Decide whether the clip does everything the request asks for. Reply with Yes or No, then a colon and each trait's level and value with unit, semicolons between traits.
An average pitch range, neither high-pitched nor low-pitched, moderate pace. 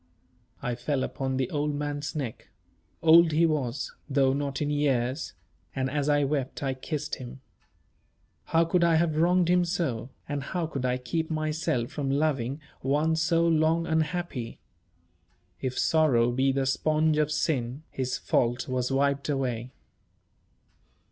Yes: average, 3.3 semitones; medium, 145 Hz; average, 150 wpm